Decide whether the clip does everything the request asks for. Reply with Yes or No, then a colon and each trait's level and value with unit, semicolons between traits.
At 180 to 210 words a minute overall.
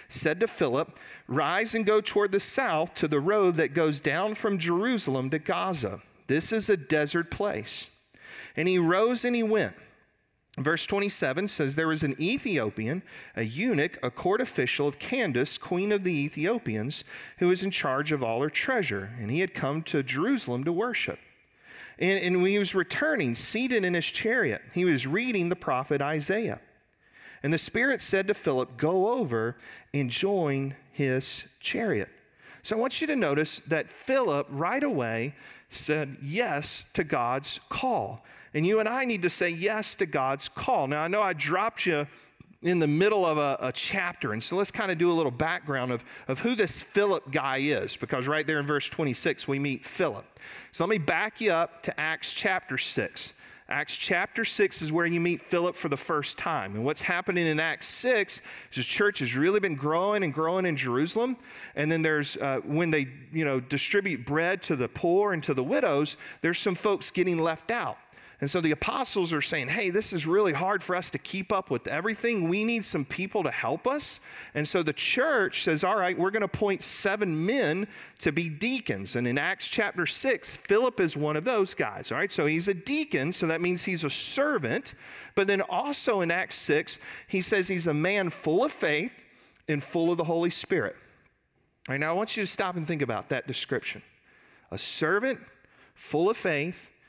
Yes: average, 200 wpm